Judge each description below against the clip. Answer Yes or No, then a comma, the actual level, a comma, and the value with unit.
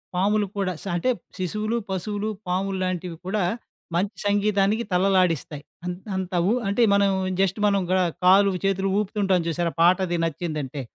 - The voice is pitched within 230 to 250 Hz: No, high, 190 Hz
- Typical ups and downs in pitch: No, narrow, 2.3 semitones